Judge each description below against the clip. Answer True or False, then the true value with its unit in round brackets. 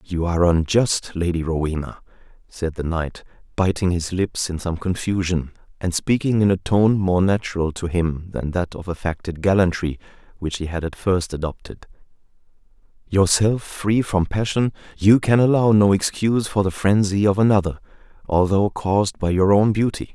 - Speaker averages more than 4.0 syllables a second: True (4.9 syllables/s)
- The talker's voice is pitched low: True (95 Hz)